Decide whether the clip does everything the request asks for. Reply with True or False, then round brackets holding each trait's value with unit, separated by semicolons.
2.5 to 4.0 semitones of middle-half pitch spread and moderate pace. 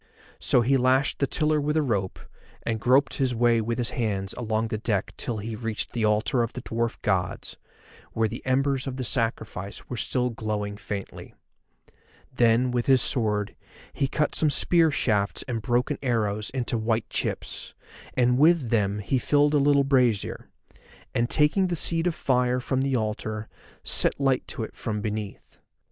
True (3.7 semitones; 175 wpm)